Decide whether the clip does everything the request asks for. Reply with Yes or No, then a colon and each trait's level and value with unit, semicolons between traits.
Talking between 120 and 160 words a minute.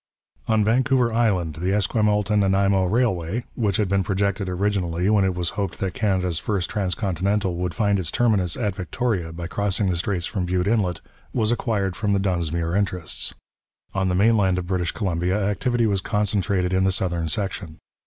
No: average, 175 wpm